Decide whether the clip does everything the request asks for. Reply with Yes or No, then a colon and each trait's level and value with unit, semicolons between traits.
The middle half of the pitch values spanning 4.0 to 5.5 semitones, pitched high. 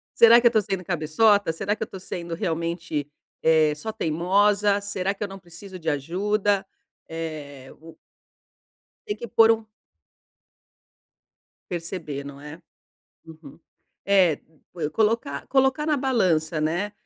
No: average, 4.7 semitones; medium, 180 Hz